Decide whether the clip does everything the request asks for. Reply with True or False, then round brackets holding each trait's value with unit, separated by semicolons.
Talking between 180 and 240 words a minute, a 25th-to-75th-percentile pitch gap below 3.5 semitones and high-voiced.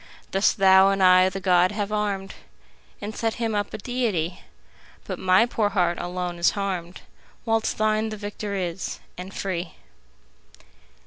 False (155 wpm; 2.5 semitones; 195 Hz)